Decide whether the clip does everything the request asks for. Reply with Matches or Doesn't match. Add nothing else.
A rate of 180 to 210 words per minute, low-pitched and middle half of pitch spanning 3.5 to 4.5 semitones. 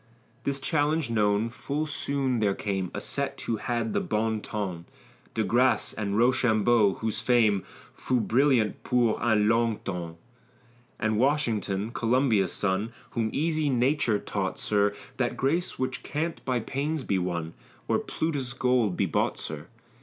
Doesn't match